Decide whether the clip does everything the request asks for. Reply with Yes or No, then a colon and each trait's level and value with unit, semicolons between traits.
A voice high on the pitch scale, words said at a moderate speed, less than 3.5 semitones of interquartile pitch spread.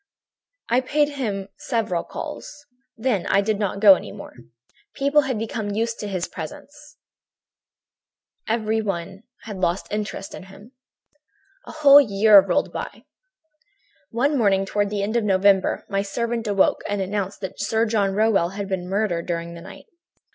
Yes: high, 205 Hz; average, 155 wpm; average, 2.9 semitones